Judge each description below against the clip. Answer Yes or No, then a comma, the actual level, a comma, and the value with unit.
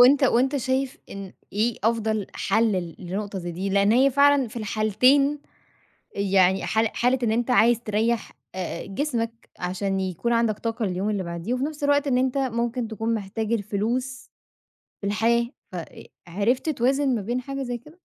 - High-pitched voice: Yes, high, 230 Hz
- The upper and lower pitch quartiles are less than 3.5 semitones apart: No, average, 4.2 semitones